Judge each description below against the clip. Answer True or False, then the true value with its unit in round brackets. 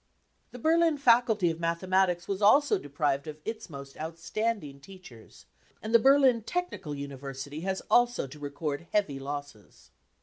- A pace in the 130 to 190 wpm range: True (140 wpm)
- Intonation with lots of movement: True (8.1 semitones)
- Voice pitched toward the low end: False (170 Hz)